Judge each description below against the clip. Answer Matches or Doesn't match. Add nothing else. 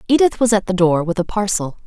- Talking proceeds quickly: Matches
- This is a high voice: Matches